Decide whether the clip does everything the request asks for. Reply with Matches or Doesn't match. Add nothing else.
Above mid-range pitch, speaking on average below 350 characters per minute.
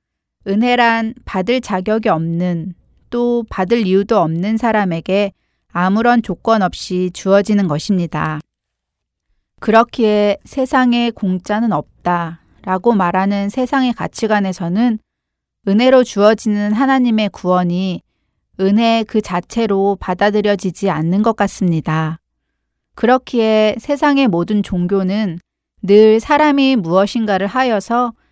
Matches